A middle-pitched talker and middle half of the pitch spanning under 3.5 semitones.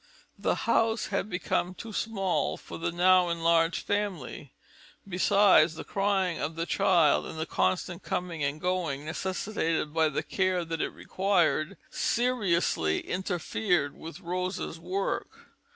Yes: medium, 180 Hz; average, 2.9 semitones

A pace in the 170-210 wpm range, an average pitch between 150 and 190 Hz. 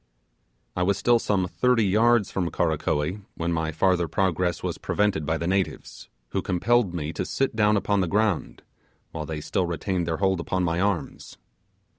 No: average, 175 wpm; very low, 90 Hz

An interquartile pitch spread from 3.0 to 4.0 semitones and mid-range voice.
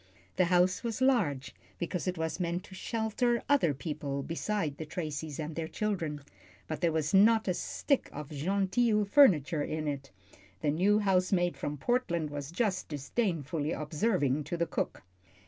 No: average, 5.3 semitones; medium, 170 Hz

